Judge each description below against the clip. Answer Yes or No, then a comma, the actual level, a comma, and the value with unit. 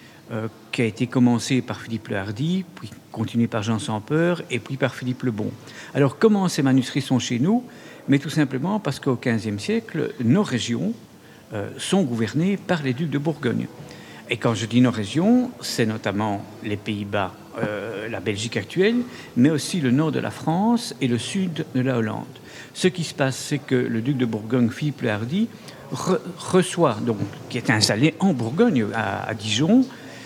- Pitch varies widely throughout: Yes, wide, 6.2 semitones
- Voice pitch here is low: Yes, low, 130 Hz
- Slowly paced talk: No, average, 190 wpm